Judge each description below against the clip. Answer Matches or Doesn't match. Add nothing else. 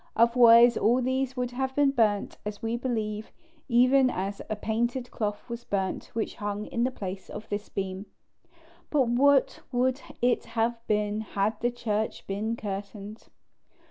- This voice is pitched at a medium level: Doesn't match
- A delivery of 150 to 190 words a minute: Matches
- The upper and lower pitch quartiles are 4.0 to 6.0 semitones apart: Doesn't match